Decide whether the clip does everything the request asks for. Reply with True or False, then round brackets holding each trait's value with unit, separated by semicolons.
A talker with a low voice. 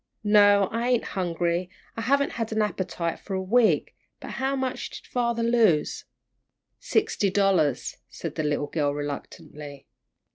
False (195 Hz)